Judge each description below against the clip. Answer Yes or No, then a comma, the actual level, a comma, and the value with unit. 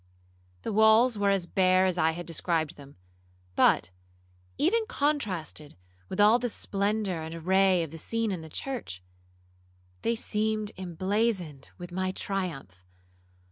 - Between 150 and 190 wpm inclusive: No, average, 140 wpm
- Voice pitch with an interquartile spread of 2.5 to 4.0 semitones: No, average, 4.9 semitones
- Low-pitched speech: No, high, 190 Hz